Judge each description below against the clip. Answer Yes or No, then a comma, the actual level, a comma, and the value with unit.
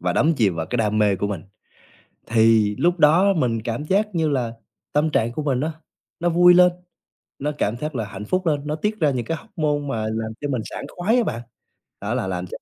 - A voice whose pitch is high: No, medium, 140 Hz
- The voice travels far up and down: Yes, wide, 6.8 semitones